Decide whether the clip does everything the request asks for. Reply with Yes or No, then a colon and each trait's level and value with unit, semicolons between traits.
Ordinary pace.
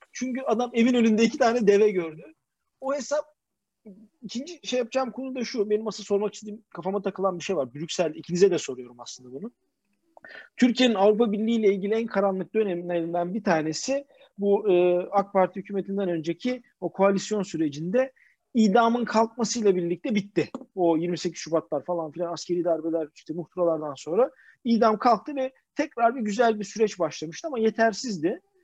No: fast, 155 wpm